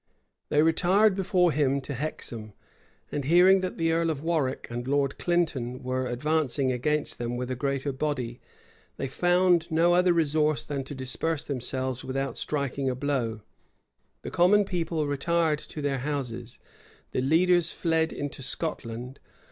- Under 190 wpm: Yes, average, 150 wpm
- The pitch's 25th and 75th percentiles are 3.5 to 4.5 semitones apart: Yes, average, 4.2 semitones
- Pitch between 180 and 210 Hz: No, medium, 145 Hz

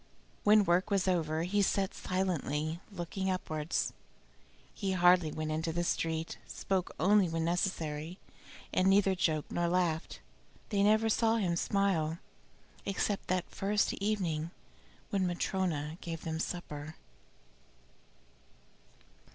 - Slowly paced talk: Yes, slow, 120 wpm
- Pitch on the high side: No, medium, 180 Hz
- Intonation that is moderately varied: Yes, average, 3.2 semitones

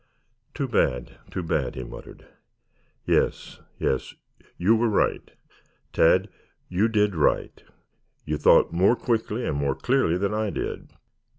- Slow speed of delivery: Yes, slow, 130 wpm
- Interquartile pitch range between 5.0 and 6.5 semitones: Yes, wide, 5.6 semitones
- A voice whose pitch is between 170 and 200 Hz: No, low, 100 Hz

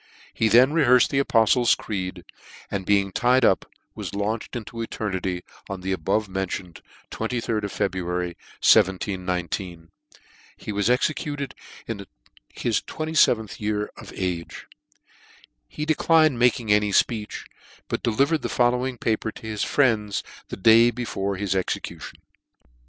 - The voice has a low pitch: Yes, low, 105 Hz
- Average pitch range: Yes, average, 4.2 semitones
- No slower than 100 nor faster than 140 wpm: Yes, slow, 135 wpm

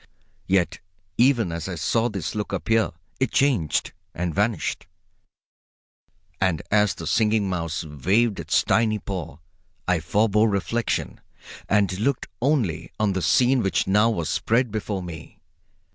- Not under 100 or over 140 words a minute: Yes, slow, 135 wpm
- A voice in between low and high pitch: No, low, 100 Hz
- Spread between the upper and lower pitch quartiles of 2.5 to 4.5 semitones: Yes, average, 4.2 semitones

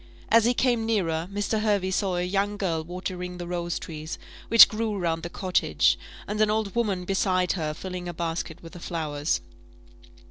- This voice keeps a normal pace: Yes, average, 180 wpm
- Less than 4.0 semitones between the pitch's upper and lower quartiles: Yes, average, 3.3 semitones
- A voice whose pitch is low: No, medium, 185 Hz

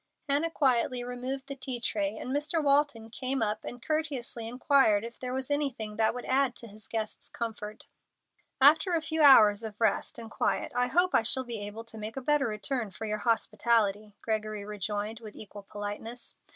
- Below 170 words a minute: No, average, 190 wpm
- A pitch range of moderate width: Yes, average, 4.0 semitones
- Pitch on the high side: Yes, high, 235 Hz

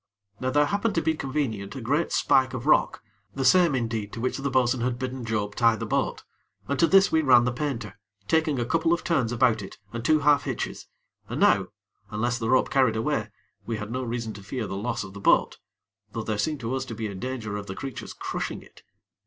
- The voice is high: No, low, 125 Hz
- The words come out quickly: Yes, fast, 230 wpm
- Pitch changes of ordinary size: Yes, average, 4.0 semitones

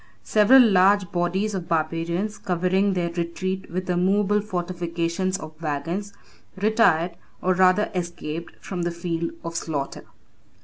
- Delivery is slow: Yes, slow, 130 wpm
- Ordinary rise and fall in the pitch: No, narrow, 2.3 semitones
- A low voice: No, medium, 180 Hz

